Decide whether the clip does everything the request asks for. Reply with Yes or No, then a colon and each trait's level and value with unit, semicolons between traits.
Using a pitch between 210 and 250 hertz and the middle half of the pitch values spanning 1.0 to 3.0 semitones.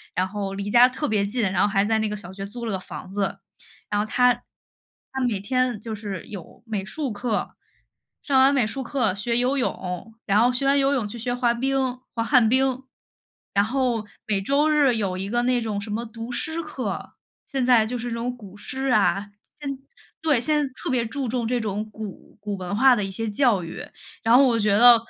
No: high, 230 Hz; average, 3.7 semitones